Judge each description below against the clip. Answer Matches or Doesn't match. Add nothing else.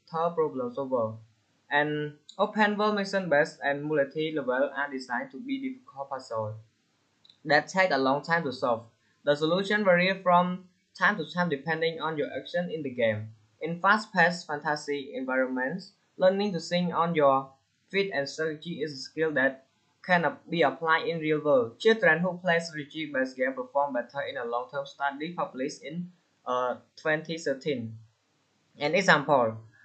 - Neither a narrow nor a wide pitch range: Matches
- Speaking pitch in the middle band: Matches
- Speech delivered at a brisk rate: Doesn't match